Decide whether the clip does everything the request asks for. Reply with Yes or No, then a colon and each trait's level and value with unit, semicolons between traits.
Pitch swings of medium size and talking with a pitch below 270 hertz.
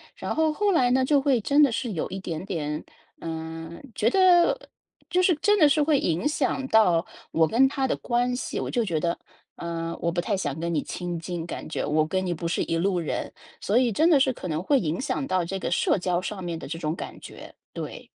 No: wide, 8.1 semitones; high, 190 Hz